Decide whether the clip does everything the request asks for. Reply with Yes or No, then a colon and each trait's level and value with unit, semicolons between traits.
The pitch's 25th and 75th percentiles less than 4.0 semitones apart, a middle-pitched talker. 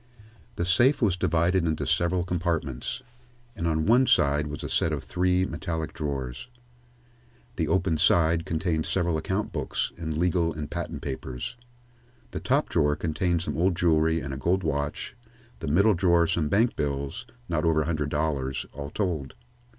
No: average, 3.1 semitones; very low, 80 Hz